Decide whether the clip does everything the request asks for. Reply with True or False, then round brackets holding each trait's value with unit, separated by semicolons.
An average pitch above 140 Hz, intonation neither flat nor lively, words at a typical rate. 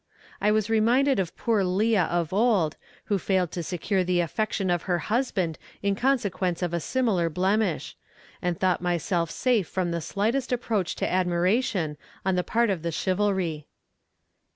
True (190 Hz; 3.8 semitones; 160 wpm)